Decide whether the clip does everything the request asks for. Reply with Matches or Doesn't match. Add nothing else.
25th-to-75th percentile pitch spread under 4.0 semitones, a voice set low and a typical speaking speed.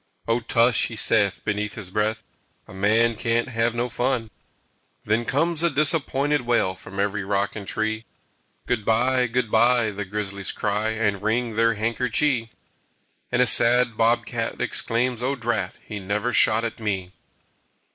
Matches